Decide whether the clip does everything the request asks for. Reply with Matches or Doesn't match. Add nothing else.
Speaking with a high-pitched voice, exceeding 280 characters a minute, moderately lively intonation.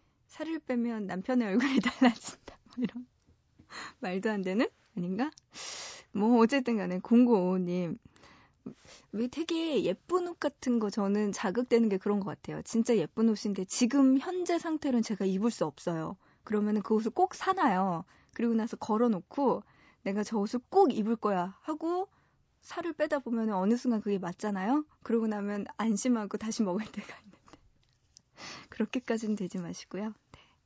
Matches